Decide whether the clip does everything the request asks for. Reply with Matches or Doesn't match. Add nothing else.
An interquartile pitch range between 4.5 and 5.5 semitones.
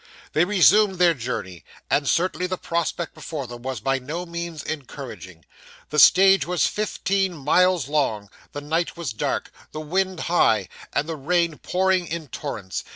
Matches